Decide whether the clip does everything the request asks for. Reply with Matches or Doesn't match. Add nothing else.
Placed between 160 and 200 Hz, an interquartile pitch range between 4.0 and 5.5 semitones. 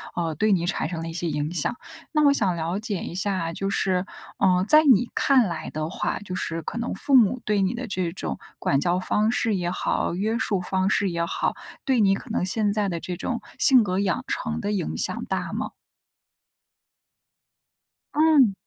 Matches